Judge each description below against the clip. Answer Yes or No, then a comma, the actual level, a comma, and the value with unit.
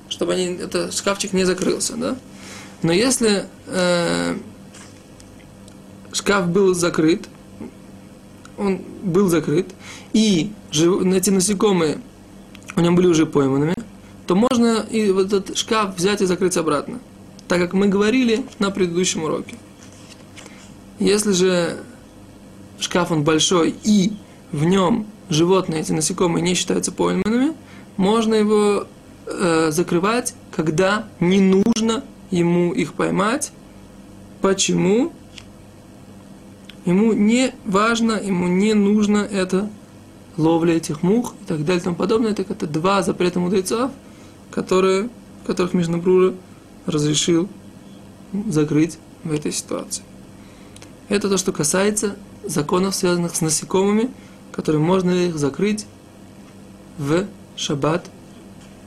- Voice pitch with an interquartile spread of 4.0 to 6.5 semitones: No, average, 3.4 semitones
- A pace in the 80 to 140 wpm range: Yes, slow, 110 wpm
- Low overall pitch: No, medium, 185 Hz